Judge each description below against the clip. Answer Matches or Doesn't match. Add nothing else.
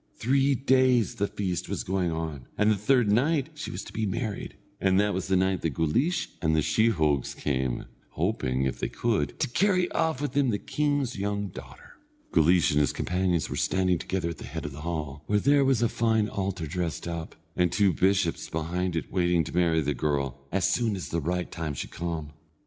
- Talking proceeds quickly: Matches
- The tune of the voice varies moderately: Doesn't match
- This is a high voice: Doesn't match